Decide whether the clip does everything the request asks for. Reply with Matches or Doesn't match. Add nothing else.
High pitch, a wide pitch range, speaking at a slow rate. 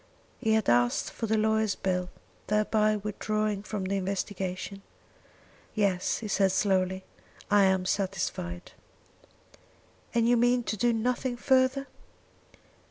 Doesn't match